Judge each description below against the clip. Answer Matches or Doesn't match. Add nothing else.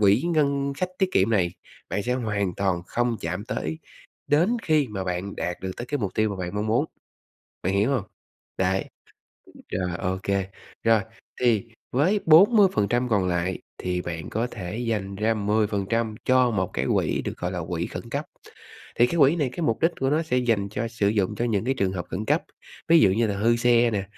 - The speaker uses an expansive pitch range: Doesn't match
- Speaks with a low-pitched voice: Matches